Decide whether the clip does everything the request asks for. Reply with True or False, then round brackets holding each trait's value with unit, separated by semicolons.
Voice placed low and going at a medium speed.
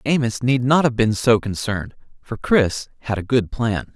True (115 Hz; 195 wpm)